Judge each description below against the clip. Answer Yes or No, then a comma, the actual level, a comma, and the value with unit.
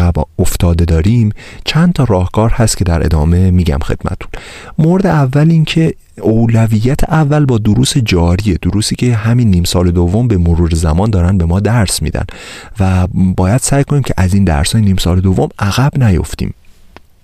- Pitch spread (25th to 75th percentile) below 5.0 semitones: No, wide, 5.4 semitones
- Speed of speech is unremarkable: No, fast, 170 wpm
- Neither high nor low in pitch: No, low, 100 Hz